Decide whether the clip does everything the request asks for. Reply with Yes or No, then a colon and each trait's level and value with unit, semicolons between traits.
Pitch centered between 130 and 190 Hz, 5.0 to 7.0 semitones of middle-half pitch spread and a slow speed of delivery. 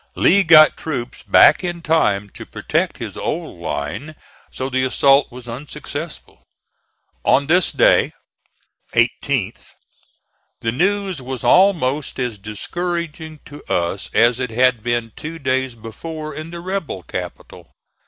Yes: medium, 140 Hz; average, 5.3 semitones; slow, 130 wpm